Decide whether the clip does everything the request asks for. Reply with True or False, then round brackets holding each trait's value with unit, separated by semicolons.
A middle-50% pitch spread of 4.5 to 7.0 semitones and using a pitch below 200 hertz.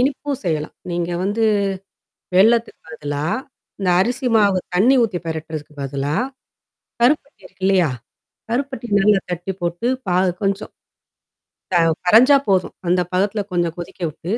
True (4.8 semitones; 190 Hz)